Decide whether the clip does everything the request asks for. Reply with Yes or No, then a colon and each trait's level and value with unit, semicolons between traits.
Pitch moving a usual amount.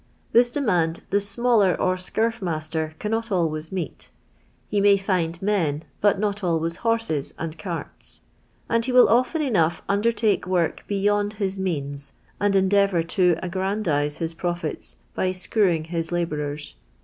Yes: average, 4.0 semitones